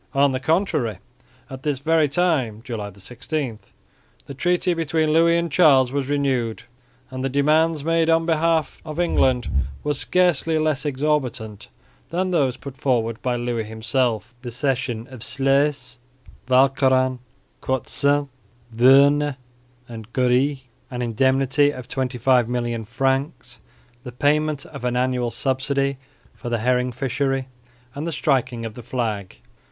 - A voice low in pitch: Yes, low, 130 Hz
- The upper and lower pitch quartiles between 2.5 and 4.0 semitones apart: Yes, average, 3.1 semitones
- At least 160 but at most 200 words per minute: No, slow, 135 wpm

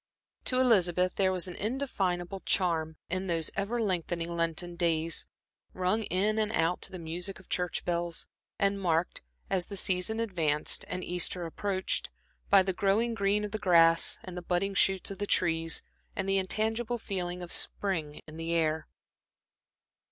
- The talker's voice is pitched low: No, medium, 185 Hz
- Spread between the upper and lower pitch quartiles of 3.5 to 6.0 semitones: No, average, 2.7 semitones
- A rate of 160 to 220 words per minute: Yes, average, 165 wpm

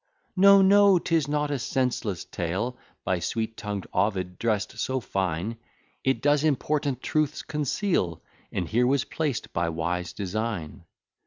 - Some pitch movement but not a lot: No, wide, 7.9 semitones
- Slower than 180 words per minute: Yes, average, 140 wpm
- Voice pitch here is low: Yes, low, 115 Hz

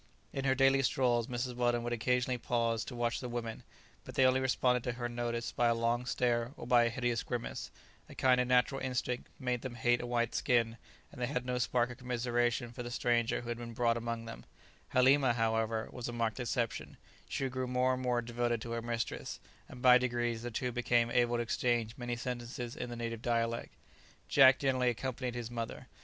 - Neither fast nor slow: No, fast, 210 wpm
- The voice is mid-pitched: No, low, 120 Hz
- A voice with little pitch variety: Yes, narrow, 1.2 semitones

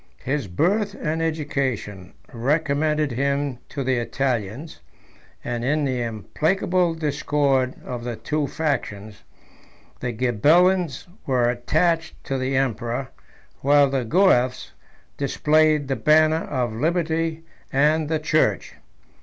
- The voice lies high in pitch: No, medium, 140 Hz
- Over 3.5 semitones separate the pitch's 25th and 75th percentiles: Yes, average, 4.3 semitones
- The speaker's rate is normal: No, slow, 110 wpm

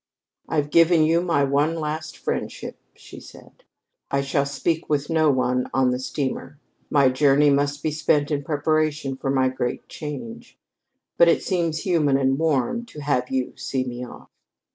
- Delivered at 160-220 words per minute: Yes, average, 165 wpm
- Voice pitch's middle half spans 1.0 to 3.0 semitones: Yes, average, 2.7 semitones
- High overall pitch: No, medium, 145 Hz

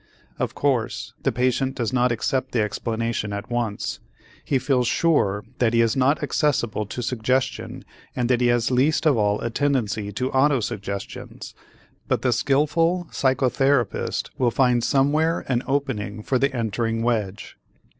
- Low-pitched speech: Yes, low, 125 Hz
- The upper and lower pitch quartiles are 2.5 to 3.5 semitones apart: Yes, average, 3.1 semitones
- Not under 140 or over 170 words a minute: Yes, average, 150 wpm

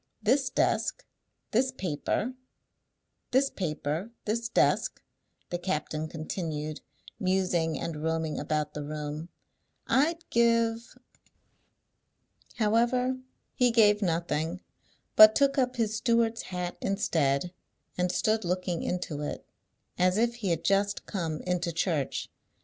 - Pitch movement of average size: No, wide, 6.2 semitones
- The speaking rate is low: Yes, slow, 115 wpm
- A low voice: No, medium, 185 Hz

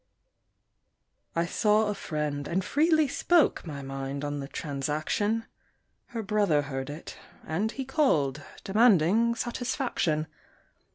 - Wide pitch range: Yes, wide, 7.8 semitones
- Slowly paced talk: Yes, slow, 115 wpm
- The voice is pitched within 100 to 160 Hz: No, medium, 175 Hz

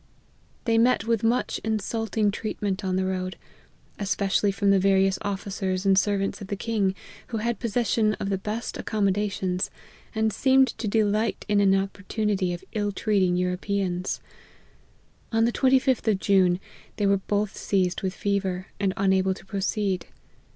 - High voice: Yes, high, 200 Hz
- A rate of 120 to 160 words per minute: Yes, average, 155 wpm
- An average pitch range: No, narrow, 2.2 semitones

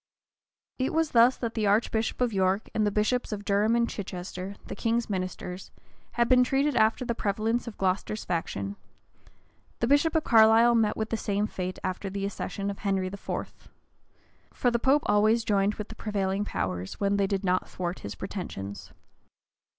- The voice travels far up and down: No, average, 3.4 semitones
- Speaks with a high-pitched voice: Yes, high, 210 Hz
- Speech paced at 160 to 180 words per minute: Yes, average, 175 wpm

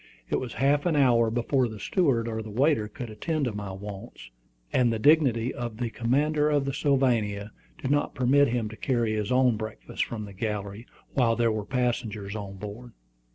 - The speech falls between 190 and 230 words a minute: Yes, average, 195 wpm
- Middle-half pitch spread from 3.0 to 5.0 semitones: Yes, average, 3.8 semitones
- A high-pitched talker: No, low, 115 Hz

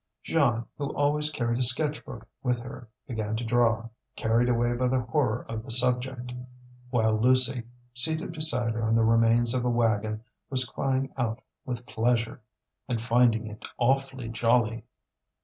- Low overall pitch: Yes, low, 120 Hz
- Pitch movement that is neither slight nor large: No, narrow, 2.1 semitones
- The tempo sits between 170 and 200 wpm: No, average, 160 wpm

